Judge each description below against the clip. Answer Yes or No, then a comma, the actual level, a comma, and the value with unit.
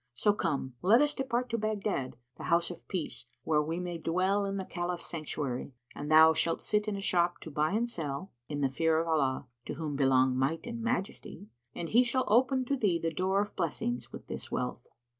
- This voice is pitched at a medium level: Yes, medium, 170 Hz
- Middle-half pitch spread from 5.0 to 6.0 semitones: Yes, wide, 5.6 semitones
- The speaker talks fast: Yes, fast, 215 wpm